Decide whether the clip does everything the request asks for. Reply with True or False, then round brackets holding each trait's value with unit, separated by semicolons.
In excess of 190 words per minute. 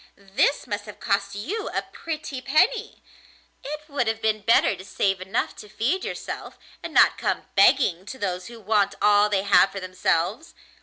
False (175 wpm)